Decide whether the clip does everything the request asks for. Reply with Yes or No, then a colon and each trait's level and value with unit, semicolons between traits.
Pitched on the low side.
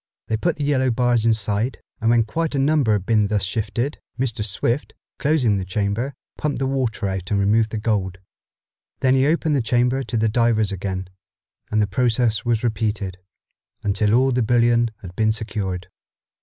Yes: low, 115 Hz